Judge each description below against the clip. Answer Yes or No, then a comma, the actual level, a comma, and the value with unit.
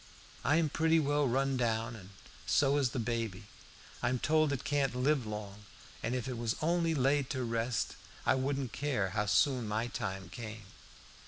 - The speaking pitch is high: No, low, 125 Hz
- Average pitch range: Yes, average, 4.2 semitones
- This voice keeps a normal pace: Yes, average, 165 wpm